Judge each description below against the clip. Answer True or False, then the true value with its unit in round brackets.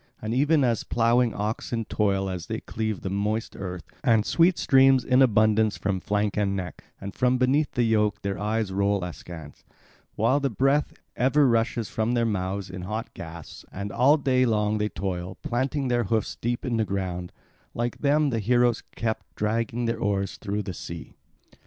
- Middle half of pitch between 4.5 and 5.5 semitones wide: False (3.7 semitones)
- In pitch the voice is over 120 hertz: False (110 Hz)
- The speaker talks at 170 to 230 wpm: True (180 wpm)